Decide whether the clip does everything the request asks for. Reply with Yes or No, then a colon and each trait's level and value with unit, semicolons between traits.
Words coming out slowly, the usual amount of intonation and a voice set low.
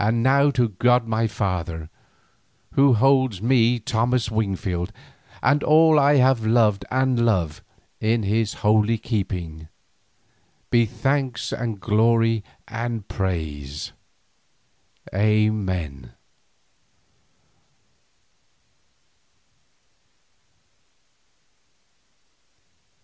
Yes: slow, 75 wpm; average, 4.0 semitones; low, 110 Hz